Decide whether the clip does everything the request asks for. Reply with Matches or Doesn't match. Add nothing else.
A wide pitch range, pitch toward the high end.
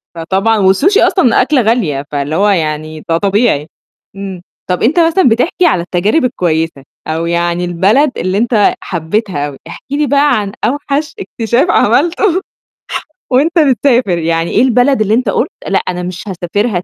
Matches